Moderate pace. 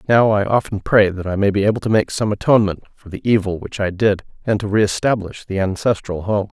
No: fast, 230 wpm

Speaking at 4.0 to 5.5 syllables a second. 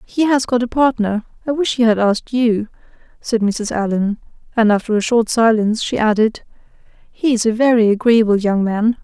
Yes: 5.3 syllables/s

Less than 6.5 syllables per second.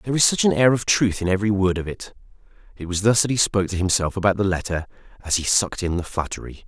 No: 7.0 syllables/s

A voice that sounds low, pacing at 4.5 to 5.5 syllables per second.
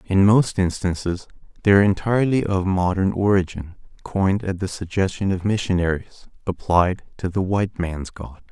Yes: very low, 95 Hz; 5.3 syllables/s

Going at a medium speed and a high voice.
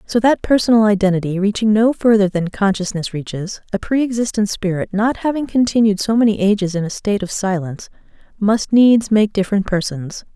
Yes: average, 175 wpm; high, 205 Hz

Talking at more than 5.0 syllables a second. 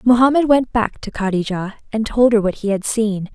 Yes: 5.2 syllables/s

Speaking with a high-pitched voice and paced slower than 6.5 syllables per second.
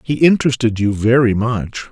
No: low, 120 Hz; 5.1 syllables/s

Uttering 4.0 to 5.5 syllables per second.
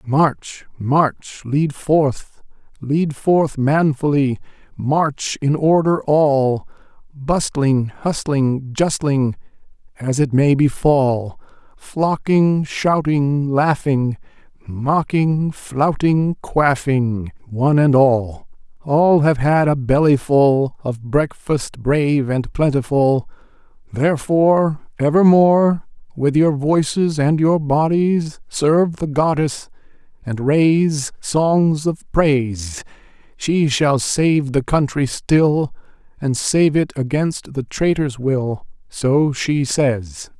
No: 3.1 syllables/s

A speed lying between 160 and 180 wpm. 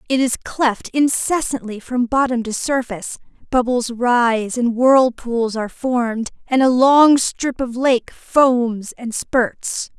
No: average, 140 wpm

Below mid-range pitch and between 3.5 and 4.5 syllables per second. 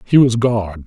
Yes: low, 110 Hz; 3.9 syllables/s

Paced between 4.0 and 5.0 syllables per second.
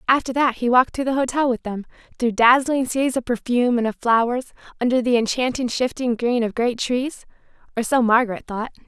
No: 5.6 syllables/s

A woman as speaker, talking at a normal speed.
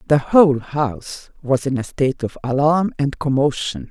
Yes: female; average, 170 wpm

